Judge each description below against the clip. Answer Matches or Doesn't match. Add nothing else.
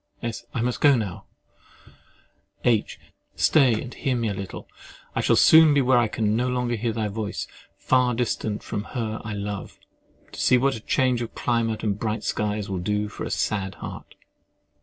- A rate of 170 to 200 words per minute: Matches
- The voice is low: Matches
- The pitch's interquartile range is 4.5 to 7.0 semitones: Doesn't match